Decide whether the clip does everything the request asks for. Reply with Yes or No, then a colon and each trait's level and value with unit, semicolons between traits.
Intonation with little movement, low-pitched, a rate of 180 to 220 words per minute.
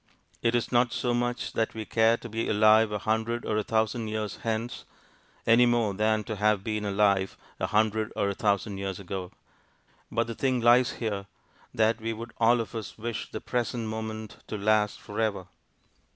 Yes: narrow, 1.7 semitones; low, 110 Hz; average, 190 wpm